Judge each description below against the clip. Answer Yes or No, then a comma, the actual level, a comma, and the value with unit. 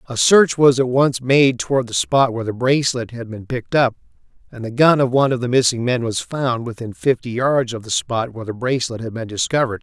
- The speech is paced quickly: Yes, fast, 240 wpm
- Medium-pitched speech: No, low, 125 Hz